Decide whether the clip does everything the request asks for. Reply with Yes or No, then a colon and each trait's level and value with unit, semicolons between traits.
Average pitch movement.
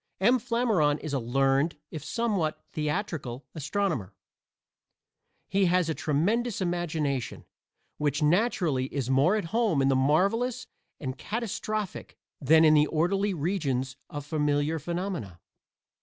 No: wide, 5.9 semitones